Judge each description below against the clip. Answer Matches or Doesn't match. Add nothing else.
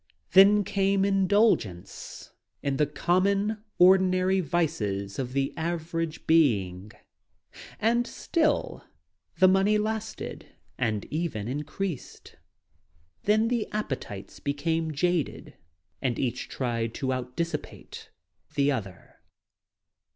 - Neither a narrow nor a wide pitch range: Doesn't match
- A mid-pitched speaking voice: Matches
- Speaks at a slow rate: Matches